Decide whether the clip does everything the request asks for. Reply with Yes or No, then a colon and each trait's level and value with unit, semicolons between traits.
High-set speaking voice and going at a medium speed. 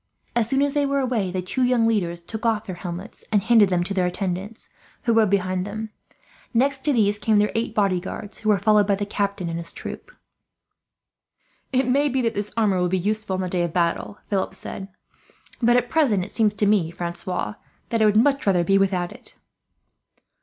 No: high, 205 Hz; fast, 210 wpm